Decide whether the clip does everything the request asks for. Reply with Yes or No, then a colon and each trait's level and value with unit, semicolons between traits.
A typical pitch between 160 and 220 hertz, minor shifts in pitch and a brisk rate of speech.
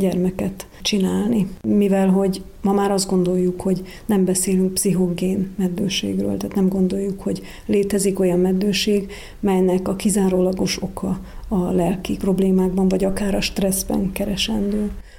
No: high, 190 Hz; narrow, 1.2 semitones; average, 125 wpm